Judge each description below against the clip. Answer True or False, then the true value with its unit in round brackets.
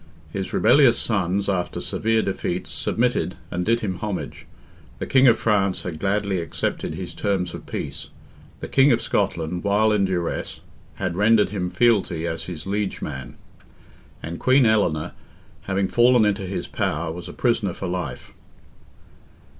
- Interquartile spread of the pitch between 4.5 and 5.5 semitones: False (3.6 semitones)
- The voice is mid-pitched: False (95 Hz)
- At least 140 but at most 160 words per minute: True (155 wpm)